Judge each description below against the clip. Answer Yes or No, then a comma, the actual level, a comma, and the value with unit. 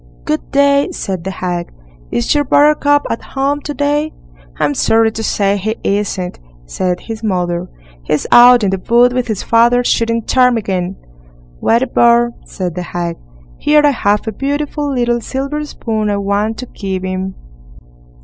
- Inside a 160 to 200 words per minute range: Yes, average, 165 wpm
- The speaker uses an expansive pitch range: Yes, wide, 5.7 semitones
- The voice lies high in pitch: Yes, high, 225 Hz